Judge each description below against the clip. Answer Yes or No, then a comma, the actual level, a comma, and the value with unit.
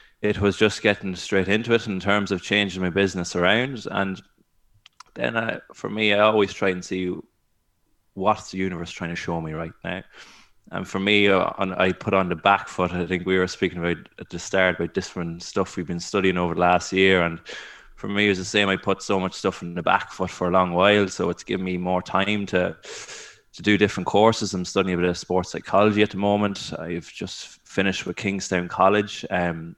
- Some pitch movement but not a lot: No, narrow, 2.3 semitones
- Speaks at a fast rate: Yes, fast, 225 wpm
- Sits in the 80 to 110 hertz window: Yes, very low, 95 Hz